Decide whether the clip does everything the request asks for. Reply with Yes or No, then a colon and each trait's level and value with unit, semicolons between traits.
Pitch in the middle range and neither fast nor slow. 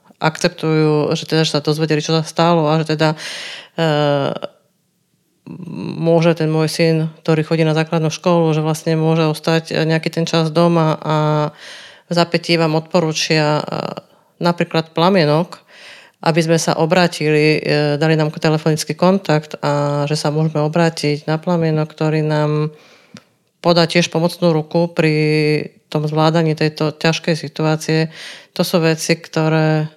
Yes: medium, 160 Hz; average, 140 wpm